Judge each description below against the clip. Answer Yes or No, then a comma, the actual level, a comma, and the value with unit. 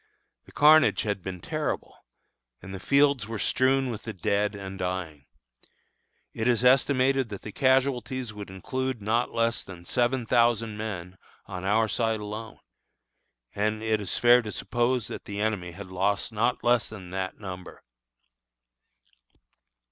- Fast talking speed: No, average, 150 wpm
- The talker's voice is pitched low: Yes, low, 110 Hz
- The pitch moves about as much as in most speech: Yes, average, 4.0 semitones